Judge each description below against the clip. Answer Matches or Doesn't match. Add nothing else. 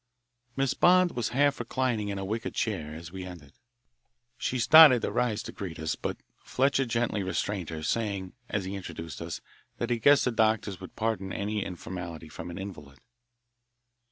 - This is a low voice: Matches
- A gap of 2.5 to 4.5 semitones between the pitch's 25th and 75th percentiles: Doesn't match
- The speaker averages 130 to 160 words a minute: Doesn't match